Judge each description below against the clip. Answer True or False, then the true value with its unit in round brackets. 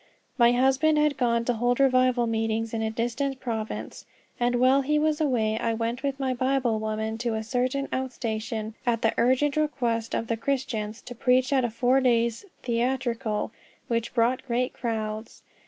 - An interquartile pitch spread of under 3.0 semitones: True (2.5 semitones)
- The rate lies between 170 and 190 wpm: True (175 wpm)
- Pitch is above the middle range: True (240 Hz)